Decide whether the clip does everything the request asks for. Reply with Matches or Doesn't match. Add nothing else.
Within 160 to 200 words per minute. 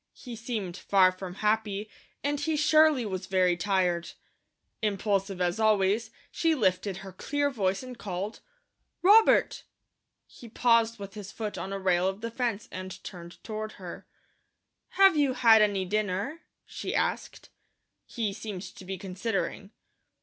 Doesn't match